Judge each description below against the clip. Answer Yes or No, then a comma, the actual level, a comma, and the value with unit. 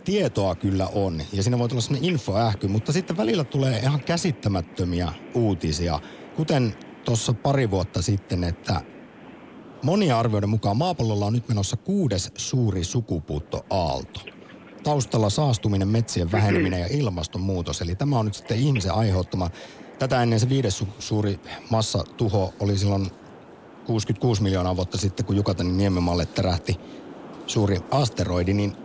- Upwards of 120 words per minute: Yes, average, 135 wpm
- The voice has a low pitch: Yes, low, 105 Hz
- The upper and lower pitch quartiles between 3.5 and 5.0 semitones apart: Yes, average, 4.6 semitones